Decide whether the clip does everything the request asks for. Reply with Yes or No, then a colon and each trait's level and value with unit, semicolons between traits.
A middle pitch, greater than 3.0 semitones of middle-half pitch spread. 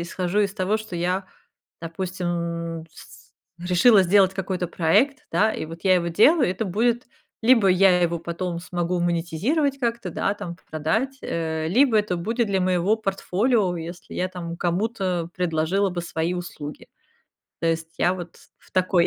Yes: medium, 180 Hz; average, 3.4 semitones